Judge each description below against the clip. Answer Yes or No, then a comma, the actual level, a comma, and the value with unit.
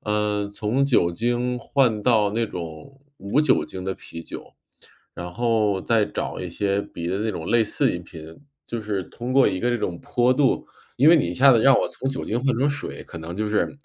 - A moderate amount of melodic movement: Yes, average, 4.9 semitones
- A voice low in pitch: Yes, low, 110 Hz